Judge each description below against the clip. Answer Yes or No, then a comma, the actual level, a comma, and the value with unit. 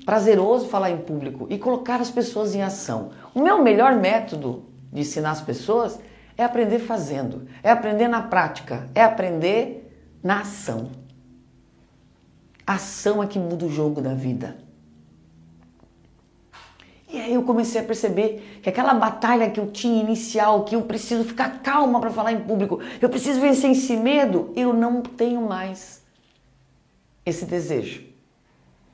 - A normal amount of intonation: No, wide, 7.2 semitones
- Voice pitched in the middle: No, high, 215 Hz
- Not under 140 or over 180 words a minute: Yes, average, 145 wpm